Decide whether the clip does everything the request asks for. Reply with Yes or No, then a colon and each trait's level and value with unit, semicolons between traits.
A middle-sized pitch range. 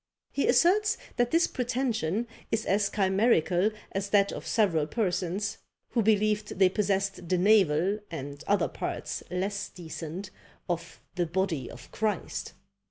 Yes: average, 3.6 semitones